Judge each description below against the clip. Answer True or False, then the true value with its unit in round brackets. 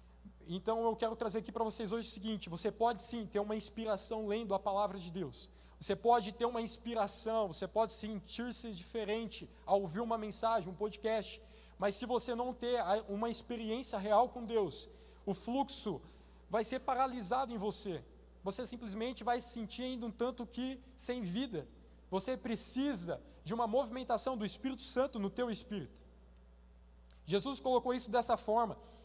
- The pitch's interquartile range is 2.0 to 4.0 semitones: True (3.0 semitones)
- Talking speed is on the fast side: False (165 wpm)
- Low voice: False (225 Hz)